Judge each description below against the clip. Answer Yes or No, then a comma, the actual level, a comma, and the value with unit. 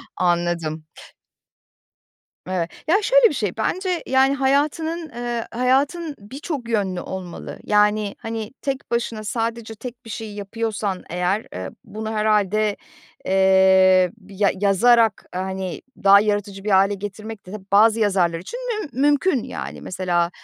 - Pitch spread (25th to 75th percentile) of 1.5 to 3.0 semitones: No, average, 4.1 semitones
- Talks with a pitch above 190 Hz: Yes, high, 210 Hz